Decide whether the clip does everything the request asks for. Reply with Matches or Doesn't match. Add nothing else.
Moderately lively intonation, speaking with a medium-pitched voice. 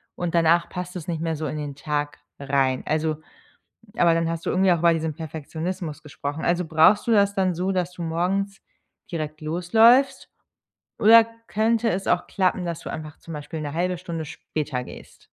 Matches